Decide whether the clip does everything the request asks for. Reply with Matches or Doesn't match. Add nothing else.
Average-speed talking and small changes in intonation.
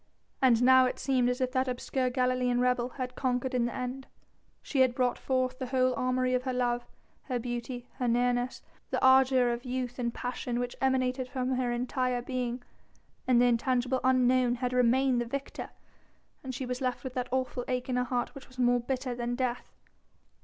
Matches